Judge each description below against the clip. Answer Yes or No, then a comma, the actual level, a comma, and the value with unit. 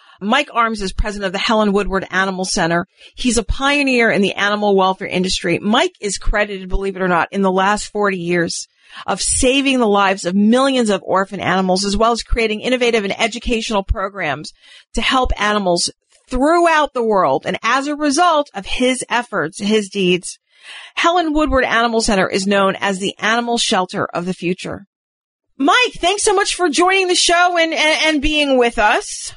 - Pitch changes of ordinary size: No, wide, 5.9 semitones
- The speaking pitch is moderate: No, high, 220 Hz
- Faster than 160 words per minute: Yes, average, 180 wpm